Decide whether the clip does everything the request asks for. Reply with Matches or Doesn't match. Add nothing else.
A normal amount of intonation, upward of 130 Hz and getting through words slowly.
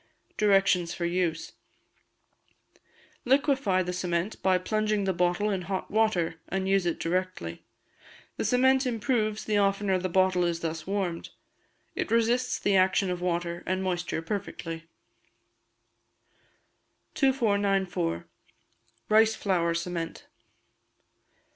Matches